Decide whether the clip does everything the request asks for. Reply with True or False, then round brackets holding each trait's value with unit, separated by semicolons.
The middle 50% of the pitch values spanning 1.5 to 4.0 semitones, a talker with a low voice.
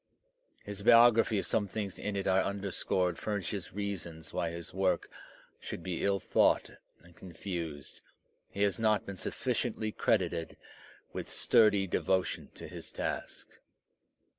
True (2.8 semitones; 95 Hz)